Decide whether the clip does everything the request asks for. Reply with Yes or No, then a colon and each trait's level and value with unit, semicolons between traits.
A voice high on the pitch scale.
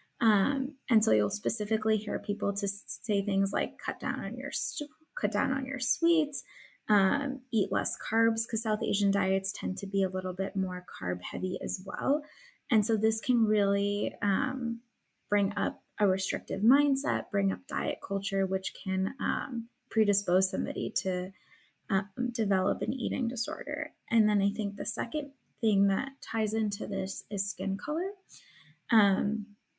Yes: high, 210 Hz